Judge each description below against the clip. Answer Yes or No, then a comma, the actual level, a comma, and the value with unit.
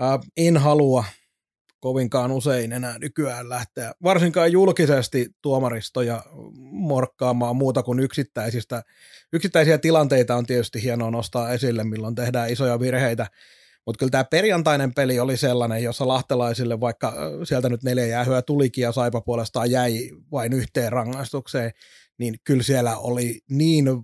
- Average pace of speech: Yes, average, 130 wpm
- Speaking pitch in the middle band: No, low, 125 Hz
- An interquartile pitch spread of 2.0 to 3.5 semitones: Yes, narrow, 2.4 semitones